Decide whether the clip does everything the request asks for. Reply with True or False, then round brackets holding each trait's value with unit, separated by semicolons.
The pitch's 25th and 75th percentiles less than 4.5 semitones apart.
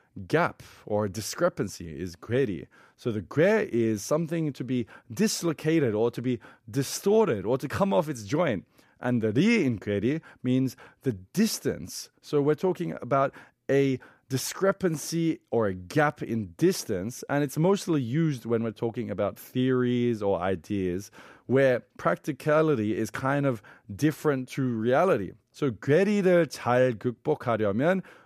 False (5.3 semitones)